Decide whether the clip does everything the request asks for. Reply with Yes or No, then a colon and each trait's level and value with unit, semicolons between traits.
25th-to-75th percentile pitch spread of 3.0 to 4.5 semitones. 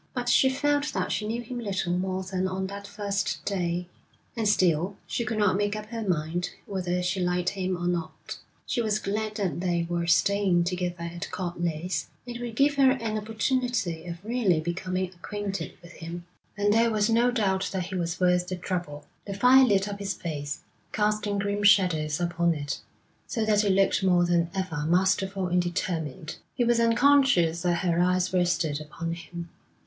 Yes: average, 3.4 semitones